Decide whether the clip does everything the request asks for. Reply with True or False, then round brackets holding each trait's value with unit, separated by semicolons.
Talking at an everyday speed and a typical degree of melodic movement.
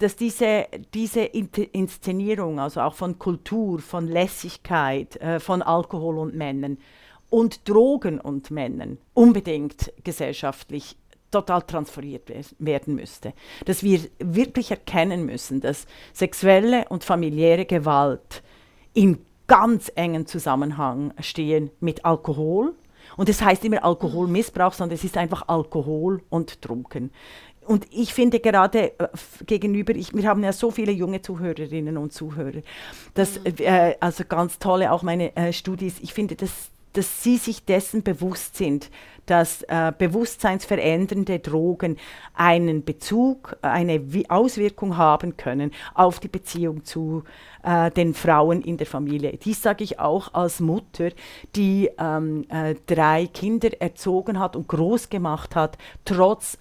True (140 wpm; 4.1 semitones)